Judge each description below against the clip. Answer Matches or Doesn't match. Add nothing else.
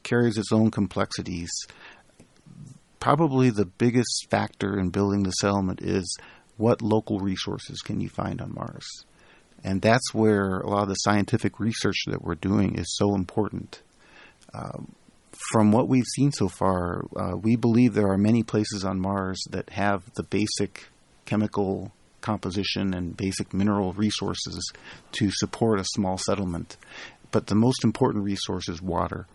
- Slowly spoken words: Doesn't match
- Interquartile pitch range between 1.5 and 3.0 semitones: Matches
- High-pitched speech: Doesn't match